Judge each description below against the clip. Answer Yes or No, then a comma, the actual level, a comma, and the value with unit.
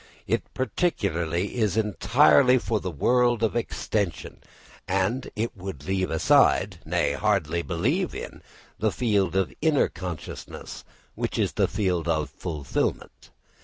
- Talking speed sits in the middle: No, slow, 130 wpm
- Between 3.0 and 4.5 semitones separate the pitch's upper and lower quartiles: No, average, 5.2 semitones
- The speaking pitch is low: Yes, very low, 95 Hz